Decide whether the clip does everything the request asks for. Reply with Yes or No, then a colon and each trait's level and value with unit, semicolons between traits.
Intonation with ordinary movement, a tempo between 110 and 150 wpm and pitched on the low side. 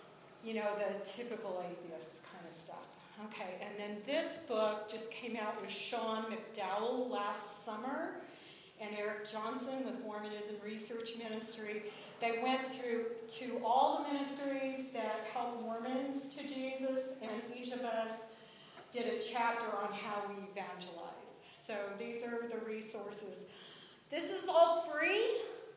No: average, 3.2 semitones; average, 140 wpm; high, 225 Hz